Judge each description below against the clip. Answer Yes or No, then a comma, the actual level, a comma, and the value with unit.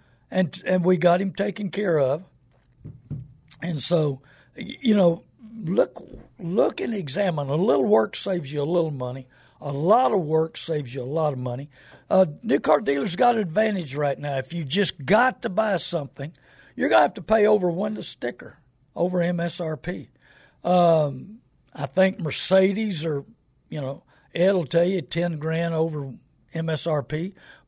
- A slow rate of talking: No, average, 165 wpm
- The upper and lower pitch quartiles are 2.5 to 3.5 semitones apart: No, average, 5.0 semitones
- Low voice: No, medium, 165 Hz